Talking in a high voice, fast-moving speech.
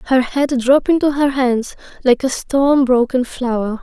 No: very high, 260 Hz; average, 170 wpm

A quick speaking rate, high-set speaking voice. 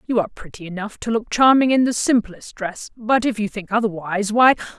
Yes: fast, 215 wpm; high, 220 Hz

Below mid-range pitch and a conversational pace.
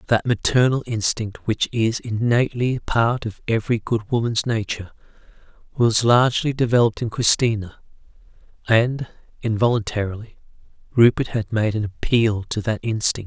No: low, 115 Hz; slow, 120 wpm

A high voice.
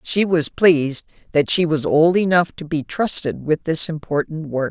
No: medium, 160 Hz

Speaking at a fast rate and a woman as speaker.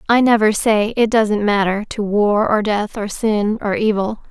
No: average, 195 wpm; female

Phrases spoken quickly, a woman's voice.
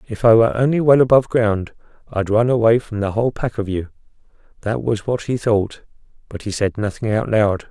No: fast, 210 wpm; male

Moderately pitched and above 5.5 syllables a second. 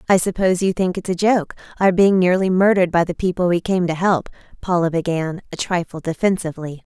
Yes: medium, 180 Hz; 6.0 syllables/s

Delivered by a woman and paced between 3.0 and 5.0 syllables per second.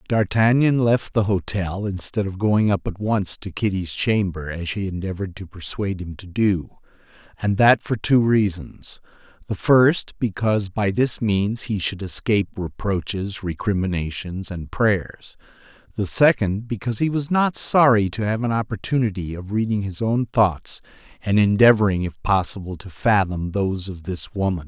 No: male; 4.7 syllables/s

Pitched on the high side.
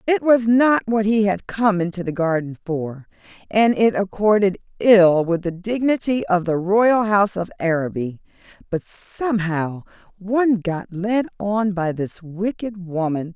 Yes: high, 195 Hz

